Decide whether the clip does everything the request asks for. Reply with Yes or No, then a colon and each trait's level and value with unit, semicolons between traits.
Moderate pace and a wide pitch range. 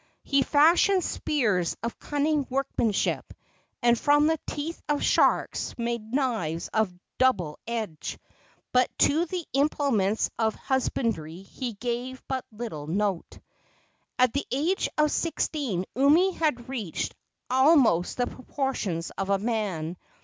No: slow, 125 wpm; wide, 5.7 semitones